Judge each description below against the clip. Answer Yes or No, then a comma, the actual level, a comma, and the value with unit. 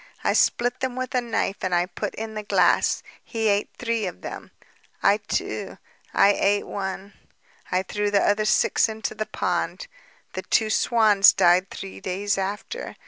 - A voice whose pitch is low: No, high, 205 Hz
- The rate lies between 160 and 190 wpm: Yes, average, 170 wpm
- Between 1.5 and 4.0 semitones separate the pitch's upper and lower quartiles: Yes, narrow, 2.4 semitones